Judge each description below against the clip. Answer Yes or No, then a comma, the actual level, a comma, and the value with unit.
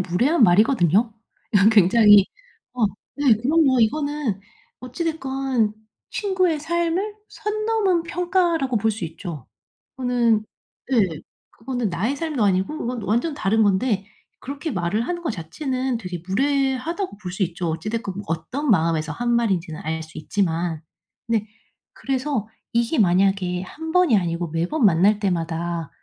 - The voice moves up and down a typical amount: No, wide, 7.7 semitones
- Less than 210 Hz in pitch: No, high, 225 Hz